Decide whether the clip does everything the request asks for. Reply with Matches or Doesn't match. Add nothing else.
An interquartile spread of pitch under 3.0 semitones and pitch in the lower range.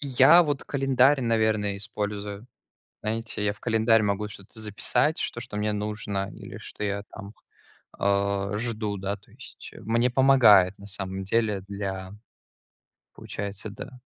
Matches